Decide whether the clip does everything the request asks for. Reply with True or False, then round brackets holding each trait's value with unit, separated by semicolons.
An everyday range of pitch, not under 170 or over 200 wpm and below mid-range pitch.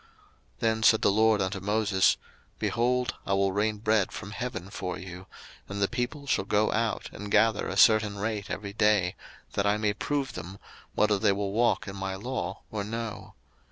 False (2.2 semitones; 190 wpm; 105 Hz)